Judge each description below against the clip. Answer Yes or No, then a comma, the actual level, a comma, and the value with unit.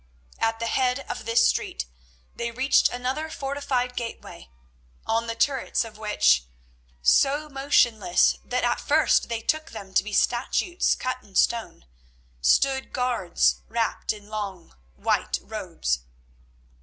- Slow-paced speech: Yes, slow, 130 wpm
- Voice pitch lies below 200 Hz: No, high, 235 Hz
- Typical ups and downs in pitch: Yes, average, 3.9 semitones